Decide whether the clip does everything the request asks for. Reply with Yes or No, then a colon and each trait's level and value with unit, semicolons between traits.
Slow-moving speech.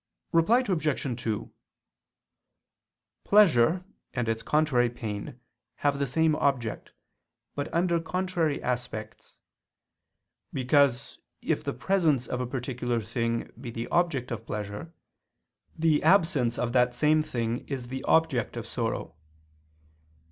Yes: slow, 120 wpm